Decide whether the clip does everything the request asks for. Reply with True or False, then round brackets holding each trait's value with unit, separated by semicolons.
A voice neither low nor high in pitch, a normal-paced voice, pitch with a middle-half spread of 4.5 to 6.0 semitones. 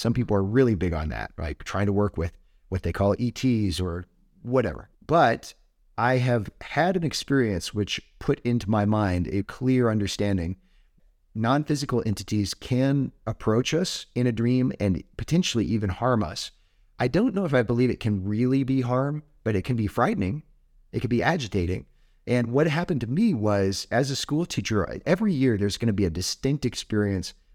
False (110 Hz; 185 wpm; 4.8 semitones)